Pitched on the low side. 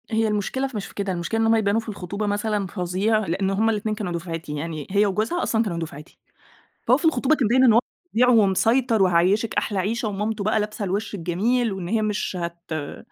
No: high, 210 Hz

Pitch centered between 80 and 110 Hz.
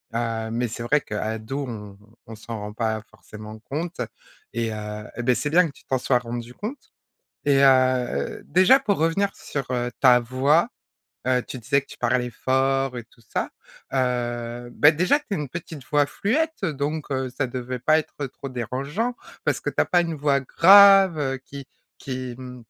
No: low, 130 Hz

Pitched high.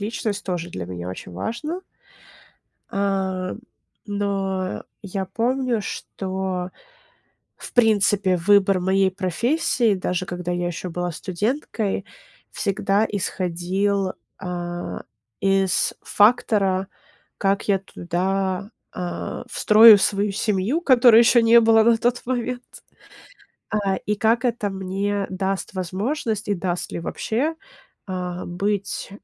Yes: high, 195 Hz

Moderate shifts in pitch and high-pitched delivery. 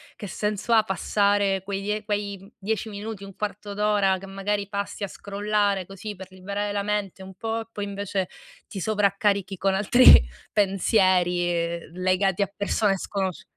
No: narrow, 1.5 semitones; high, 200 Hz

